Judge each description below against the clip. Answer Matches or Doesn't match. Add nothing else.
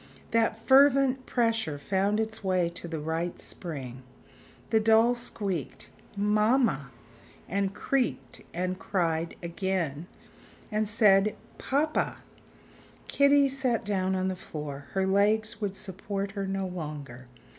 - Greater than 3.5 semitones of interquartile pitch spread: Matches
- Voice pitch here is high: Matches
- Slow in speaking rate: Matches